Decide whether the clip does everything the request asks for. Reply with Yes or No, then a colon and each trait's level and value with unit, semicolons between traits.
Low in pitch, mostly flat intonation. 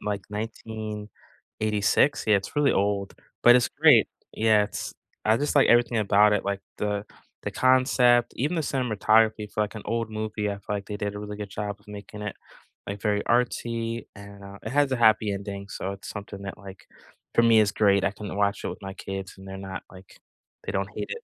Yes: low, 105 Hz; narrow, 2.3 semitones